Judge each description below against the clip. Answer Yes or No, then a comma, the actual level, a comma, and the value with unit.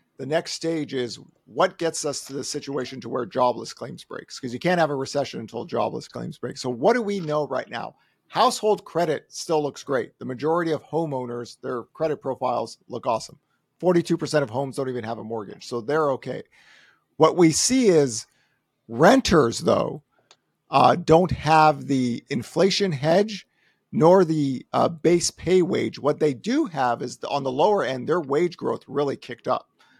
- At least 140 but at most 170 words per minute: No, average, 180 wpm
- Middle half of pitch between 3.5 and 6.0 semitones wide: Yes, average, 4.5 semitones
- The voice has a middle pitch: Yes, medium, 150 Hz